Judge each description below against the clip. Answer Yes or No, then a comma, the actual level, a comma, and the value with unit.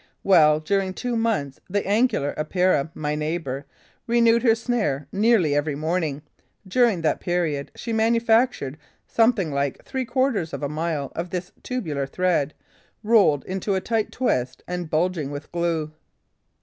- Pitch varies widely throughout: Yes, wide, 6.8 semitones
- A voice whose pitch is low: No, medium, 180 Hz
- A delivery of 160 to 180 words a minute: No, average, 145 wpm